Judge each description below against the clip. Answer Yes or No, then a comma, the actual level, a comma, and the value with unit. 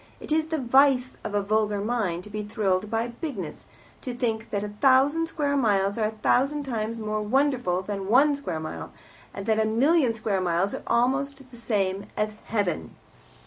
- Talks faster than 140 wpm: Yes, average, 185 wpm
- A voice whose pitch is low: No, high, 220 Hz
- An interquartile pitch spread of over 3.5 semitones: Yes, average, 4.6 semitones